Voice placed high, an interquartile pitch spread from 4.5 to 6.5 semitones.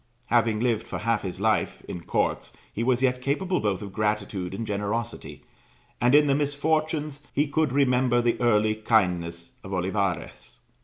No: low, 115 Hz; average, 5.2 semitones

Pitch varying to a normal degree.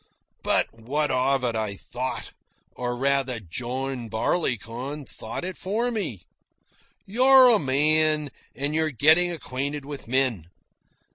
Yes: average, 4.2 semitones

